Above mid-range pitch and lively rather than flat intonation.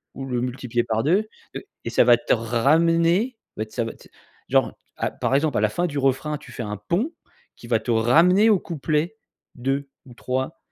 No: low, 135 Hz; wide, 5.8 semitones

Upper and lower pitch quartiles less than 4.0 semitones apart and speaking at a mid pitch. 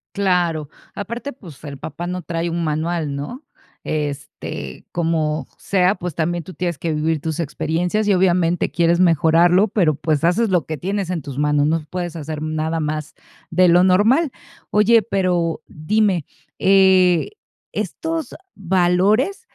Yes: average, 3.3 semitones; medium, 175 Hz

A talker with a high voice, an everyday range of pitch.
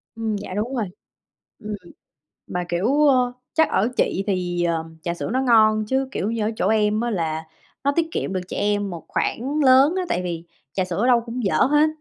No: high, 215 Hz; wide, 5.7 semitones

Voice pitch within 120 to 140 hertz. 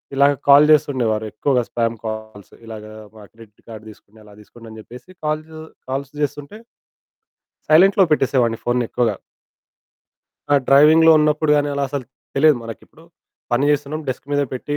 Yes: low, 135 Hz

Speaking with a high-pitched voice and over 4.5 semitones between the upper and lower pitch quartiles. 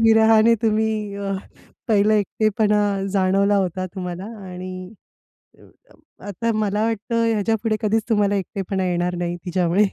No: high, 205 Hz; average, 2.7 semitones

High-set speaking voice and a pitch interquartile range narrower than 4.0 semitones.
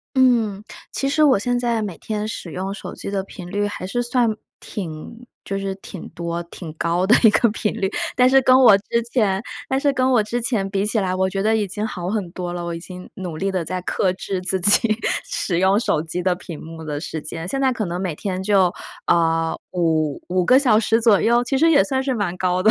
No: high, 195 Hz; average, 4.5 semitones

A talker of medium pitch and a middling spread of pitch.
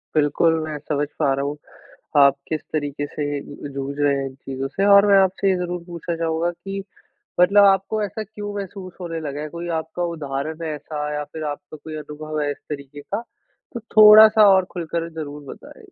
Yes: medium, 160 Hz; average, 4.6 semitones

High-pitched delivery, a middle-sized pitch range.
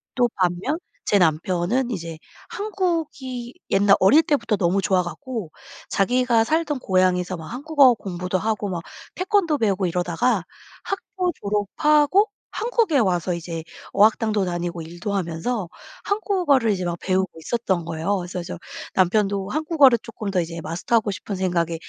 No: high, 200 Hz; wide, 6.6 semitones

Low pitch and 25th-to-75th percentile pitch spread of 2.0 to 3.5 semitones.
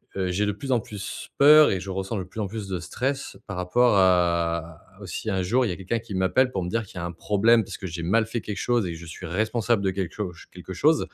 No: very low, 95 Hz; average, 4.1 semitones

